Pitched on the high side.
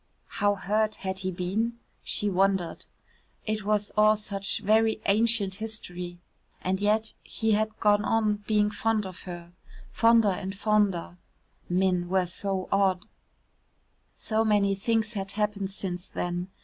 Yes: high, 205 Hz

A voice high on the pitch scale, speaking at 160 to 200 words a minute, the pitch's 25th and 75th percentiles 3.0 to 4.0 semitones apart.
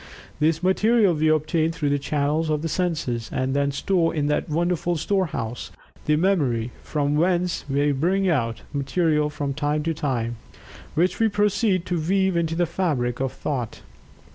No: medium, 155 Hz; average, 165 wpm; average, 3.7 semitones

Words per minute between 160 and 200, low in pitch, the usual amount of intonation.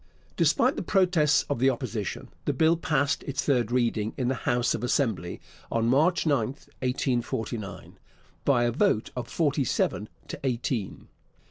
No: average, 150 wpm; low, 125 Hz; average, 3.4 semitones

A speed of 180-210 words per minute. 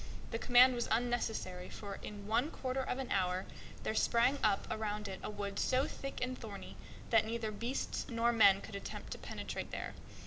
Yes: average, 185 wpm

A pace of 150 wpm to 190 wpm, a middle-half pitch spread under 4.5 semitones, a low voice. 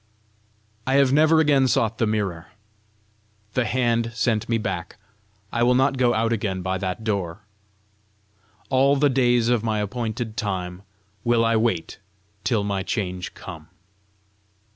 No: average, 140 wpm; average, 3.8 semitones; low, 115 Hz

